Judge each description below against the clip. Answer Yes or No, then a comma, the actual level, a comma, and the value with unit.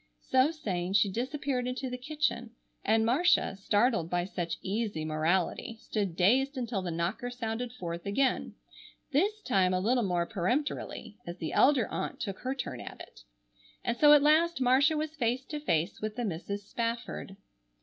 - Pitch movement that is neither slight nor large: No, wide, 5.8 semitones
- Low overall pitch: No, high, 230 Hz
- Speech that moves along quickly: No, average, 170 wpm